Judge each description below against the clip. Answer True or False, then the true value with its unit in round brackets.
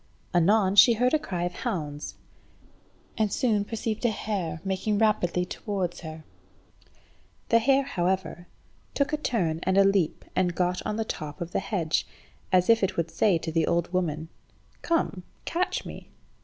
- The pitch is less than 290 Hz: True (190 Hz)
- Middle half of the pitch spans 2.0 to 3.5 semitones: False (4.1 semitones)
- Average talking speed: True (165 wpm)